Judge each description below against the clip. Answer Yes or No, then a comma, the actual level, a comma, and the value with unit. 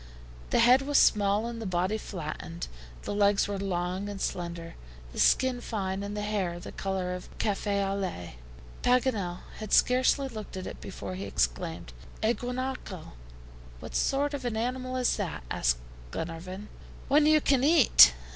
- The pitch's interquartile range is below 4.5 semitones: No, wide, 5.4 semitones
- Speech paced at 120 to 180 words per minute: Yes, average, 165 wpm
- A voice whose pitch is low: No, high, 205 Hz